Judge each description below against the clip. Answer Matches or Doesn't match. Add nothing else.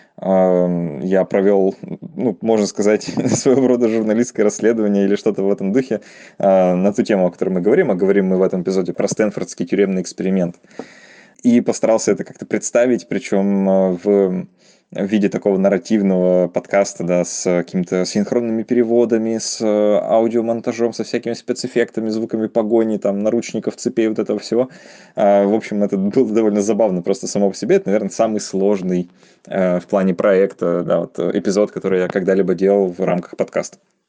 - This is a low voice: Matches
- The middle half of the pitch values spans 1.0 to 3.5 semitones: Matches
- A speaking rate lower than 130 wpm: Doesn't match